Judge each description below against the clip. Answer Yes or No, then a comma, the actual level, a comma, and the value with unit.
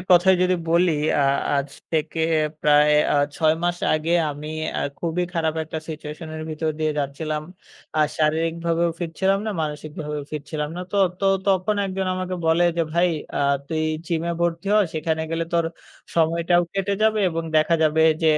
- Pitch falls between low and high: Yes, medium, 165 Hz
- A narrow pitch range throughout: Yes, narrow, 2.2 semitones